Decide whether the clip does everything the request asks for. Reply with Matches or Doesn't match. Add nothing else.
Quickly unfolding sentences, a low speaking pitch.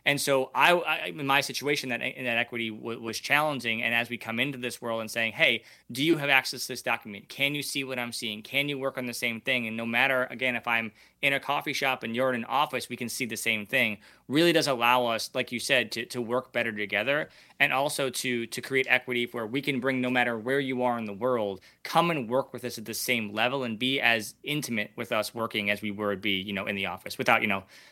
Matches